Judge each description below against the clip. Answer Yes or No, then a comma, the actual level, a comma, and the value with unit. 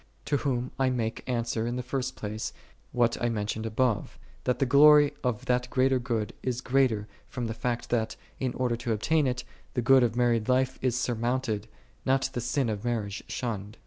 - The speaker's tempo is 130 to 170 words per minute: No, average, 190 wpm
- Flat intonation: Yes, narrow, 2.3 semitones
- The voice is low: Yes, low, 120 Hz